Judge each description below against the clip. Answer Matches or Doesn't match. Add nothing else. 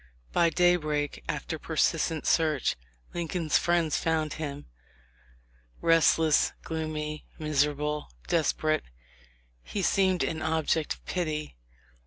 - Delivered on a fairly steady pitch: Matches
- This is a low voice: Doesn't match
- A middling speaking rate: Doesn't match